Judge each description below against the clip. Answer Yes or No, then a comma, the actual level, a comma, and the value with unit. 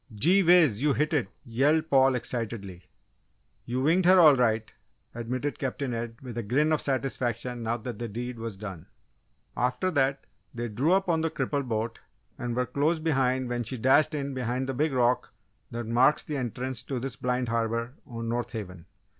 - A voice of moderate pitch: No, low, 125 Hz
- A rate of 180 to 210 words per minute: Yes, average, 185 wpm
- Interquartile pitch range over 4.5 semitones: No, average, 3.3 semitones